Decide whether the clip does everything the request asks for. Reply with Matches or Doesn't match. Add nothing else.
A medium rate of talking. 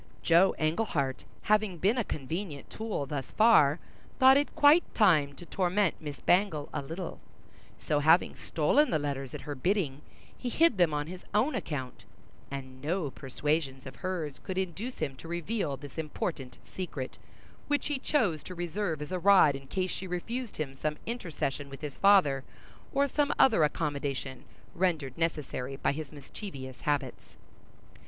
Matches